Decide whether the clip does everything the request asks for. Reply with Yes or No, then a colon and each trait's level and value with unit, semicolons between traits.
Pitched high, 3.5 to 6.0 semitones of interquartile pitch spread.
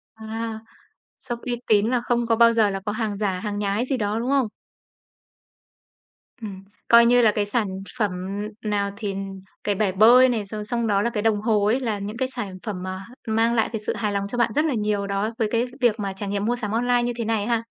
No: high, 220 Hz; narrow, 2.5 semitones